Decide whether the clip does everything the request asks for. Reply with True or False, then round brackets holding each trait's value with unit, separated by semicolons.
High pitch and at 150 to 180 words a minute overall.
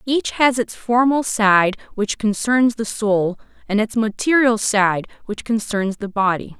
True (220 Hz; 155 wpm)